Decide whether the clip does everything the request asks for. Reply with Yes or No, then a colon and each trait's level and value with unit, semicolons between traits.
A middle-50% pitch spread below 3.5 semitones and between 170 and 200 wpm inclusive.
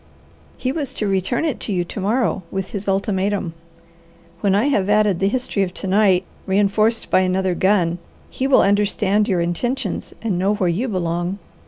Yes: narrow, 2.4 semitones; average, 180 wpm